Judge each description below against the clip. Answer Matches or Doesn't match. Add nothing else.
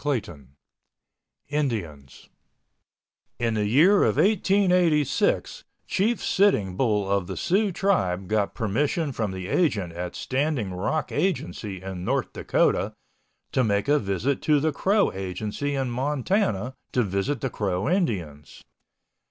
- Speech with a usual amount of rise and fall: Doesn't match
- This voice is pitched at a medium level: Doesn't match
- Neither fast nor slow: Doesn't match